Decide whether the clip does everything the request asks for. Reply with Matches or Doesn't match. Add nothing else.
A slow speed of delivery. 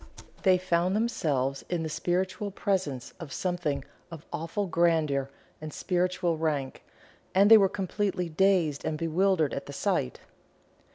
Matches